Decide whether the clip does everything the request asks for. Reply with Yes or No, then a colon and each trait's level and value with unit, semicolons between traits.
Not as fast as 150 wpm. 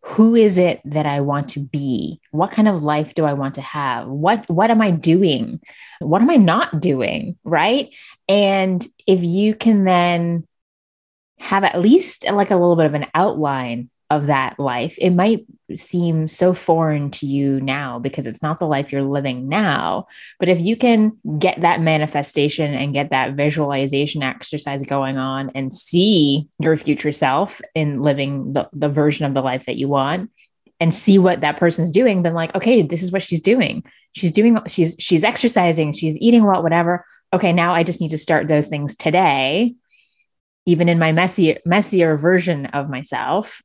No: average, 185 wpm